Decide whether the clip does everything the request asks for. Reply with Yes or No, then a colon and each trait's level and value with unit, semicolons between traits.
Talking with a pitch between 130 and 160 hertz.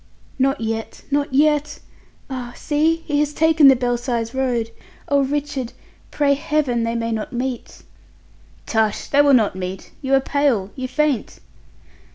No: very high, 265 Hz